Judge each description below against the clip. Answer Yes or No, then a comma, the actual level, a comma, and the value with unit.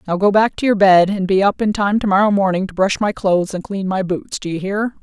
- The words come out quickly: Yes, fast, 300 wpm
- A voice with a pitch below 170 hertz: No, high, 195 Hz